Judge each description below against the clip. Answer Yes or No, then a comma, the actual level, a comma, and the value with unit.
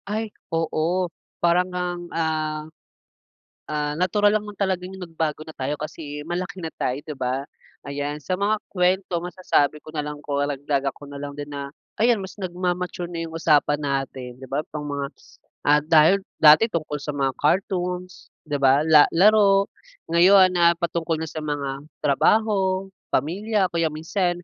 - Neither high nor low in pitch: Yes, medium, 165 Hz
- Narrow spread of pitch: No, average, 3.8 semitones